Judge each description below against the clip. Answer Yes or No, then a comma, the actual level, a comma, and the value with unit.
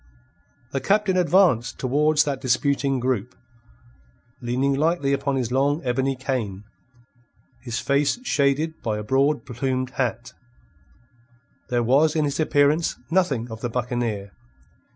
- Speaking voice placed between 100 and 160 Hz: Yes, low, 135 Hz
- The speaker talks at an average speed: No, slow, 125 wpm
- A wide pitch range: No, average, 3.2 semitones